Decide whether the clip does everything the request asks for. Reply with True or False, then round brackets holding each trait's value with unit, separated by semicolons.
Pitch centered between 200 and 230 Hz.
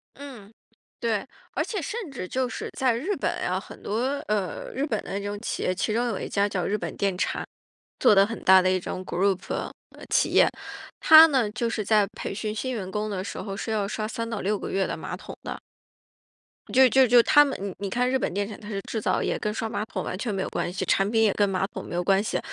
True (210 Hz)